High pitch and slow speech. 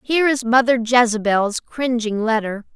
Yes: high, 235 Hz; slow, 130 wpm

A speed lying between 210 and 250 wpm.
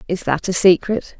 No: average, 200 wpm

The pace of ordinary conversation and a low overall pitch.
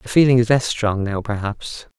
No: fast, 210 wpm; low, 115 Hz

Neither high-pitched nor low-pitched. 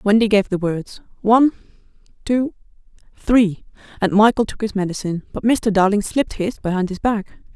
No: high, 210 Hz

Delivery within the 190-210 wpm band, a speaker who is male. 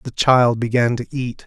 Yes: fast, 205 wpm; male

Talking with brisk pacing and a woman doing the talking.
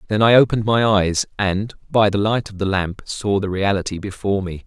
No: fast, 220 wpm; male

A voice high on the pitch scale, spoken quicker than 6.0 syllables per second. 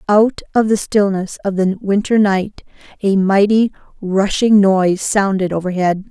No: high, 200 Hz; 4.4 syllables/s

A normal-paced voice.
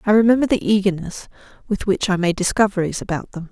Yes: average, 190 wpm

